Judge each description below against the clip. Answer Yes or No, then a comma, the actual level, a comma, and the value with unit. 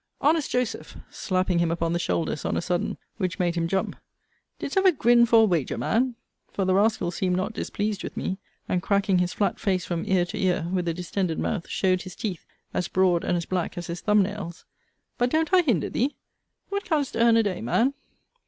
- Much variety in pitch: No, average, 4.4 semitones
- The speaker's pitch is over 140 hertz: Yes, high, 190 Hz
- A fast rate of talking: Yes, fast, 210 wpm